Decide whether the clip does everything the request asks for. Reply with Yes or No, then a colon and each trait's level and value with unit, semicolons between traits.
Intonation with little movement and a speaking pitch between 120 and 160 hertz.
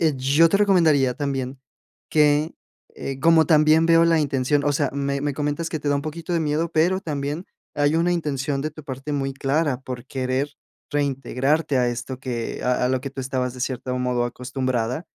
No: average, 3.1 semitones; medium, 140 Hz